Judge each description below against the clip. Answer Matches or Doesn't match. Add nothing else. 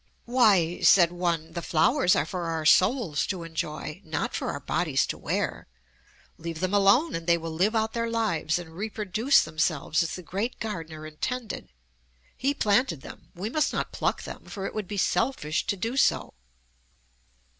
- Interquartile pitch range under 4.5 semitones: Doesn't match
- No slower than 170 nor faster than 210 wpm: Matches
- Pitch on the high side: Doesn't match